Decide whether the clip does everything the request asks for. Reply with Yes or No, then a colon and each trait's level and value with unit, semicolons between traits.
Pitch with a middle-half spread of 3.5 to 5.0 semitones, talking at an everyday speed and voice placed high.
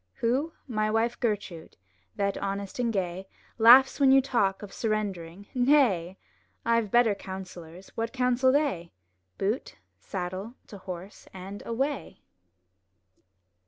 No: average, 4.4 semitones; slow, 125 wpm; high, 210 Hz